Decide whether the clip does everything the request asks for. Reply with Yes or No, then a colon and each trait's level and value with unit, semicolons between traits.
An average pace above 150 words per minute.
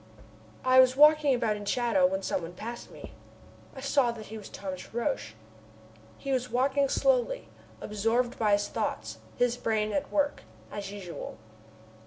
Yes: average, 165 wpm